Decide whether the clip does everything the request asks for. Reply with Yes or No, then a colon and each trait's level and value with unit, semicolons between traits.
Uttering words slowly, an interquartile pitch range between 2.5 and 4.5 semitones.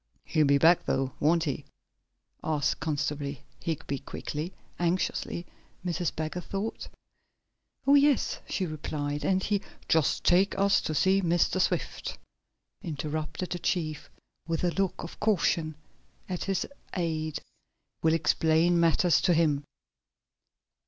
Yes: slow, 125 wpm; average, 2.9 semitones